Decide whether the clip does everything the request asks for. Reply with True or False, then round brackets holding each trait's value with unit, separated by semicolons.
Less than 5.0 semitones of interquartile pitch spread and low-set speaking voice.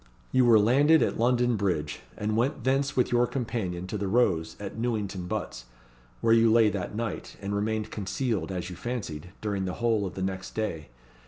True (4.1 semitones; 110 Hz)